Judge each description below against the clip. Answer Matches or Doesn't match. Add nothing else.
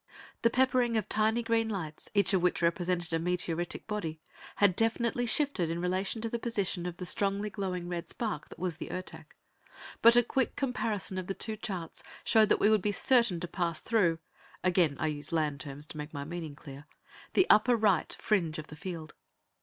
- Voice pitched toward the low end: Doesn't match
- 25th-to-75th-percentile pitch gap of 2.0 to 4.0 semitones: Doesn't match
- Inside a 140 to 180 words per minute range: Doesn't match